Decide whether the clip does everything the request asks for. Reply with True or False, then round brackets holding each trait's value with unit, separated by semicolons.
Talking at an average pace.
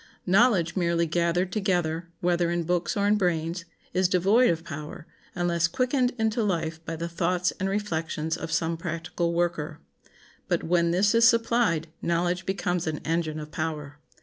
True (160 wpm)